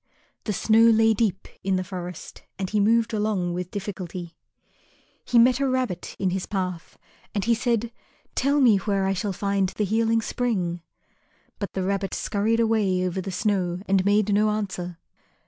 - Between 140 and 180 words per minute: Yes, average, 170 wpm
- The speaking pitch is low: No, high, 200 Hz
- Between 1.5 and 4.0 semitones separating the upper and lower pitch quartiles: Yes, average, 3.2 semitones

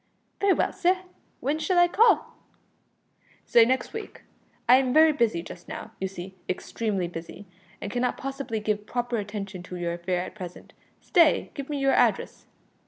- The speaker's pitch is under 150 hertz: No, high, 235 Hz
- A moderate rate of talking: Yes, average, 170 wpm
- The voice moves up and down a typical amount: No, wide, 7.1 semitones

